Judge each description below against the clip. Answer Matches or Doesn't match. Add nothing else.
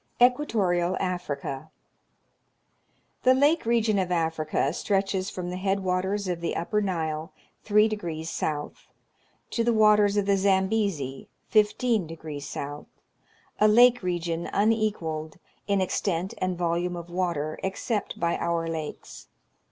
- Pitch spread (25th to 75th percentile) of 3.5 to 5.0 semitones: Matches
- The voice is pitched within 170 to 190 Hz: Matches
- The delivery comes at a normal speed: Doesn't match